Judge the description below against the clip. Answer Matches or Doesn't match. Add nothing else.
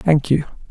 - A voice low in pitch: Doesn't match